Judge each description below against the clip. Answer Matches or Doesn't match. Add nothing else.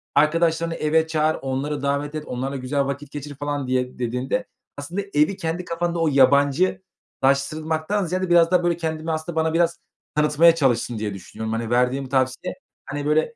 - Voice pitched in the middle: Matches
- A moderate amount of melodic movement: Matches